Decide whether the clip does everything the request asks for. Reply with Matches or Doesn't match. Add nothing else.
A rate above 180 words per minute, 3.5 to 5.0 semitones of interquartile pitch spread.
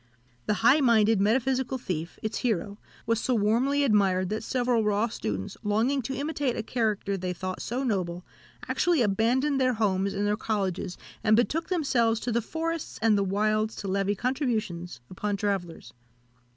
Doesn't match